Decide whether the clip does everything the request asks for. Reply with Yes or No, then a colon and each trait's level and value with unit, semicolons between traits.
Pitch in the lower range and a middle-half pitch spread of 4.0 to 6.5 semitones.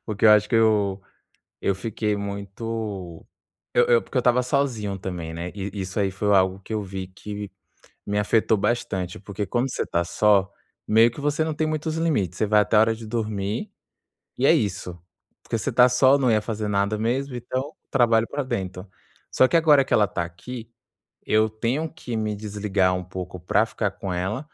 No: low, 105 Hz; average, 3.6 semitones